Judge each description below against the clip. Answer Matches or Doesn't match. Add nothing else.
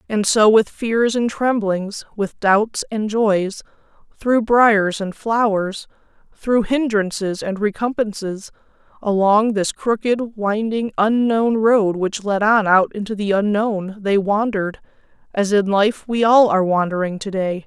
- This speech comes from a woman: Matches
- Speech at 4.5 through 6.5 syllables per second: Doesn't match